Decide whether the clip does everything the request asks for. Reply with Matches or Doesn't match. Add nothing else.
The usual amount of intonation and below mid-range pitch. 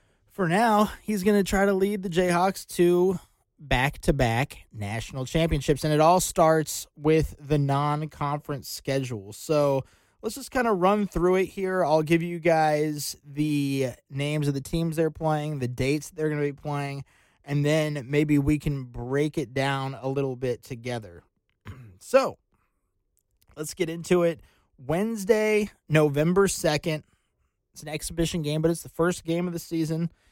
Doesn't match